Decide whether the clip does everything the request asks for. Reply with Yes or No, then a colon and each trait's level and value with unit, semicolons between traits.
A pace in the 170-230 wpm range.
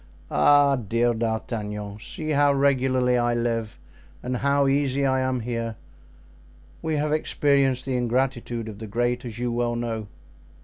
No: average, 145 wpm